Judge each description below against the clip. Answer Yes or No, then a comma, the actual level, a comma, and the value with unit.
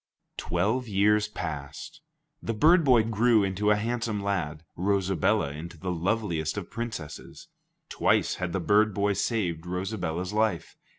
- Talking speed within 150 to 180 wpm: No, slow, 135 wpm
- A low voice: Yes, low, 100 Hz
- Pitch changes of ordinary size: Yes, average, 4.2 semitones